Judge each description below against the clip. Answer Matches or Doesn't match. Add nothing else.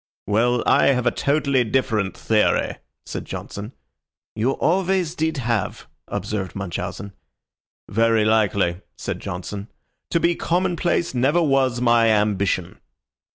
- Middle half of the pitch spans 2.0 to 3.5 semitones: Doesn't match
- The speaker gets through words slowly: Matches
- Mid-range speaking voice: Doesn't match